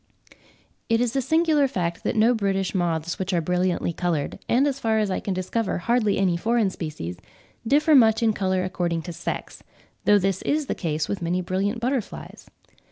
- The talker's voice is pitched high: Yes, high, 195 Hz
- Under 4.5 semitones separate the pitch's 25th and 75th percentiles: No, average, 4.8 semitones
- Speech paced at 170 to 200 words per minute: Yes, average, 185 wpm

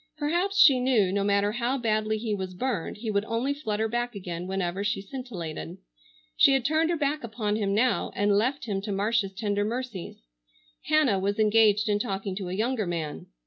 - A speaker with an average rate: Yes, average, 190 wpm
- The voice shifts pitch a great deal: No, average, 4.0 semitones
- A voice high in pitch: Yes, high, 215 Hz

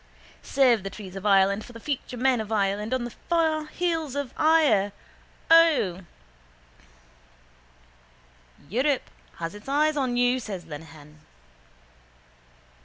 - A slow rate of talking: Yes, slow, 120 wpm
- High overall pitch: Yes, high, 240 Hz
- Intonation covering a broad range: Yes, wide, 6.6 semitones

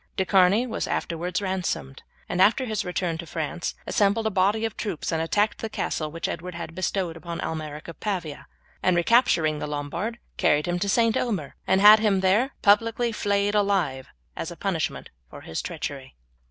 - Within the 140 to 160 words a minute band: No, average, 180 wpm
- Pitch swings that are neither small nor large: Yes, average, 4.3 semitones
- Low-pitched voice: No, medium, 185 Hz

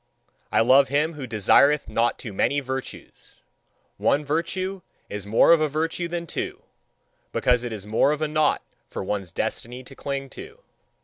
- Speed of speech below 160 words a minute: No, average, 170 wpm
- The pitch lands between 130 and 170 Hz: Yes, medium, 140 Hz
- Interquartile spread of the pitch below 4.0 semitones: No, average, 5.3 semitones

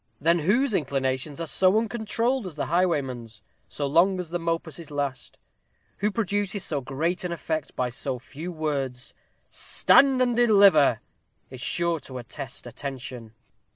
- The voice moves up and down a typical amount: No, wide, 6.0 semitones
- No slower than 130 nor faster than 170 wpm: Yes, average, 145 wpm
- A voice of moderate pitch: Yes, medium, 160 Hz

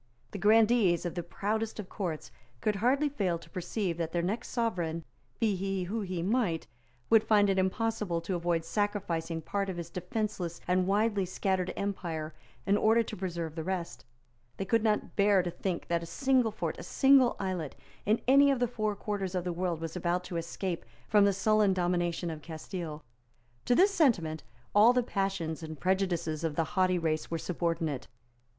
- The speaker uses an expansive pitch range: No, average, 3.9 semitones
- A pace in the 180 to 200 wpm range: Yes, average, 185 wpm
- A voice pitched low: No, medium, 185 Hz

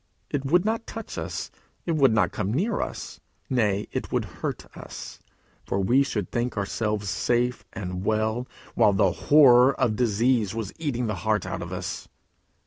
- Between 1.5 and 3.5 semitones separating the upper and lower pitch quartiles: No, average, 4.3 semitones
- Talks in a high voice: No, low, 115 Hz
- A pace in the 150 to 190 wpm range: Yes, average, 170 wpm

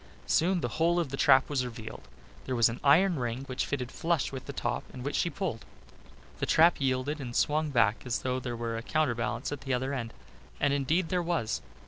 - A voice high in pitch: No, low, 135 Hz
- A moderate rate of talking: No, fast, 215 wpm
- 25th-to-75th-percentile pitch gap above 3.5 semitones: Yes, average, 4.2 semitones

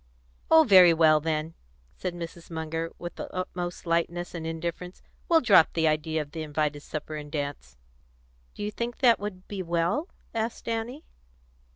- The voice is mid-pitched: Yes, medium, 170 Hz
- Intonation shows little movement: No, average, 4.1 semitones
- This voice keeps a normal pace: Yes, average, 165 wpm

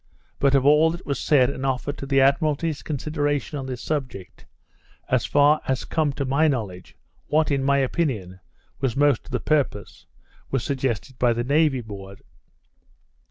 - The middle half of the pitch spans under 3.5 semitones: Yes, average, 2.7 semitones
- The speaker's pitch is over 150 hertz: No, low, 135 Hz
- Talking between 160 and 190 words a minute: Yes, average, 170 wpm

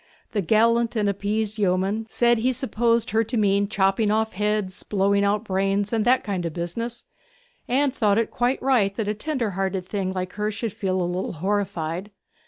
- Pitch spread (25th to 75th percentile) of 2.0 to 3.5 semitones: Yes, average, 2.9 semitones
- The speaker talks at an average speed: Yes, average, 190 wpm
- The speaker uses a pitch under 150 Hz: No, high, 210 Hz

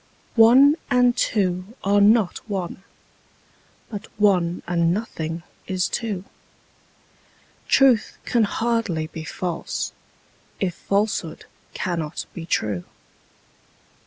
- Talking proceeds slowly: Yes, slow, 95 wpm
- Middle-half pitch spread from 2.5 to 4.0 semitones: No, average, 4.5 semitones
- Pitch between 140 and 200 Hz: Yes, high, 190 Hz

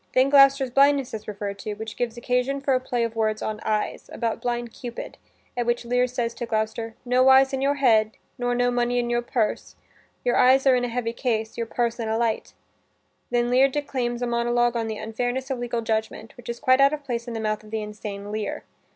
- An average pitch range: No, narrow, 2.2 semitones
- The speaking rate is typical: No, fast, 230 wpm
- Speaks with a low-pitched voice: No, high, 240 Hz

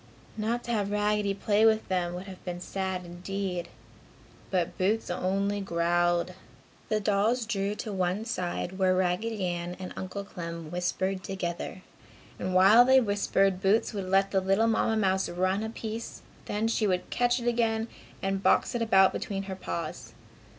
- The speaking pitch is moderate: No, high, 195 Hz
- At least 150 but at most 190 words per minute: Yes, average, 165 wpm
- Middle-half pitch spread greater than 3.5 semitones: No, average, 2.8 semitones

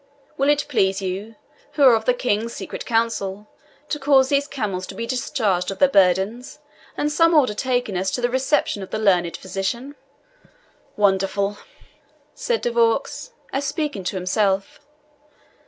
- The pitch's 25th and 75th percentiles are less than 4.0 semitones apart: No, wide, 5.6 semitones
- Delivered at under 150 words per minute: No, average, 155 wpm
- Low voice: No, high, 225 Hz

